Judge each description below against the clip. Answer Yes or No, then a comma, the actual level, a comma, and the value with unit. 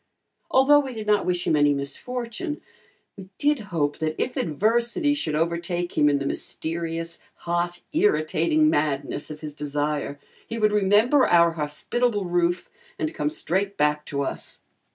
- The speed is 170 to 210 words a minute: No, average, 155 wpm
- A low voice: No, medium, 175 Hz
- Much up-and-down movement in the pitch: Yes, wide, 7.3 semitones